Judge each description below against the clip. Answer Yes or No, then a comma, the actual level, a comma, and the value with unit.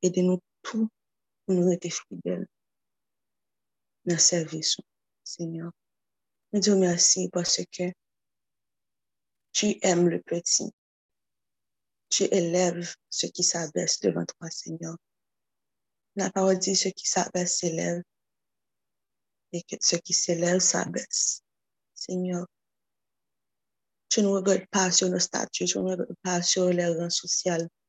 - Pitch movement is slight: Yes, narrow, 1.5 semitones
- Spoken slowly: Yes, slow, 125 wpm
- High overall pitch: No, medium, 175 Hz